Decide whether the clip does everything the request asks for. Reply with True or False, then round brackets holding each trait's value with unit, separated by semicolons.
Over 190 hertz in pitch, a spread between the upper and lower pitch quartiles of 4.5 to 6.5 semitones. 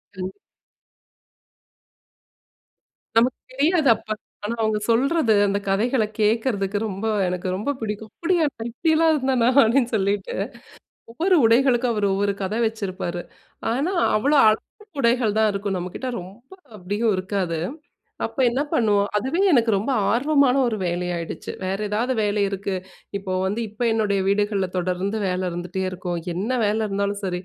False (215 Hz; 3.9 semitones)